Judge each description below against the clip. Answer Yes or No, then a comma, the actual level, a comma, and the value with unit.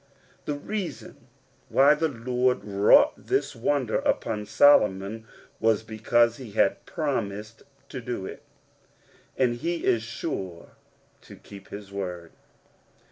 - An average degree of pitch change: Yes, average, 4.2 semitones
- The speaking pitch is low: Yes, low, 115 Hz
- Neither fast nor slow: No, slow, 120 wpm